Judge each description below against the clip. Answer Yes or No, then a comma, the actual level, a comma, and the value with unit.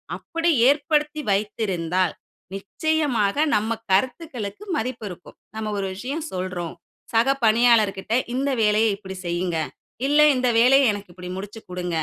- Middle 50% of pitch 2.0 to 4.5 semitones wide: No, wide, 5.5 semitones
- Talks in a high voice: Yes, high, 215 Hz